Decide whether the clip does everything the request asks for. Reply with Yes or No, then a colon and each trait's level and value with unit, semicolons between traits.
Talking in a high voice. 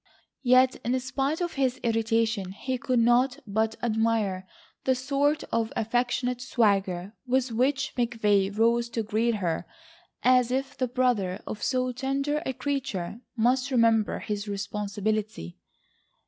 Yes: high, 235 Hz